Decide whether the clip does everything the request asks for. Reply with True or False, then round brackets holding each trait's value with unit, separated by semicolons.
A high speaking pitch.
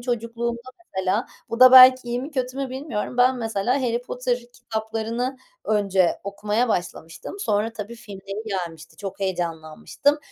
True (225 Hz)